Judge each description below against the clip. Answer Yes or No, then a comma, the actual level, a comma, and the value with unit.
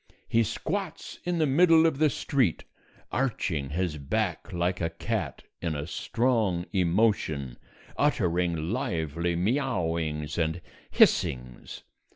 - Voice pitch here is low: Yes, very low, 90 Hz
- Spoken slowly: Yes, slow, 115 wpm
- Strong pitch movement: Yes, wide, 8.0 semitones